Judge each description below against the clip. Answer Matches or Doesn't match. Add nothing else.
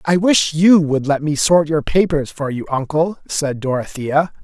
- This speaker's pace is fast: Doesn't match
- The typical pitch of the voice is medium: Matches